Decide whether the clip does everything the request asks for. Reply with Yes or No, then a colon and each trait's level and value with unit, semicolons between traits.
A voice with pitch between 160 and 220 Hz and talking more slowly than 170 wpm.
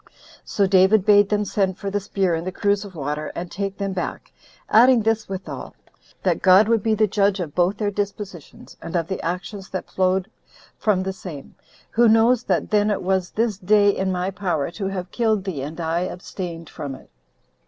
No: high, 190 Hz; average, 195 wpm